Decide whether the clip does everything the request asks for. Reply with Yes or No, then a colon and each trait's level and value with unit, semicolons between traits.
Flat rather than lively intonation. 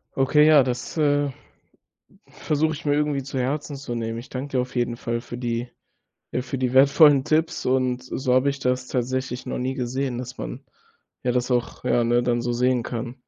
Yes: narrow, 2.3 semitones